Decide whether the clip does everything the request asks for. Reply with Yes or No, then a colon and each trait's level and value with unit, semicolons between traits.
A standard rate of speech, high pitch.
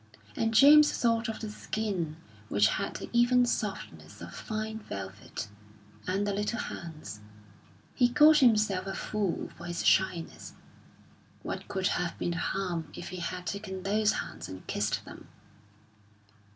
Yes: average, 150 wpm; high, 200 Hz